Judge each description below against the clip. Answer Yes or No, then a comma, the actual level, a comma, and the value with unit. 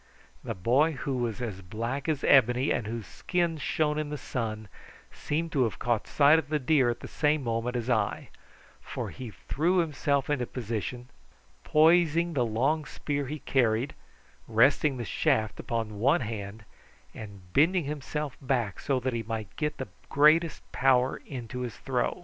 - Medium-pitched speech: No, low, 130 Hz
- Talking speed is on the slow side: No, average, 165 wpm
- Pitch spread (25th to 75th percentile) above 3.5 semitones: Yes, average, 4.6 semitones